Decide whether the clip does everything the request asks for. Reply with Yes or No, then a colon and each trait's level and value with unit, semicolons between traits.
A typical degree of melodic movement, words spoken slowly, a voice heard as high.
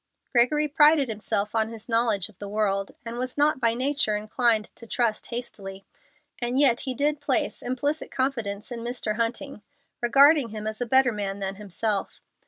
No: average, 3.8 semitones; average, 175 wpm; high, 235 Hz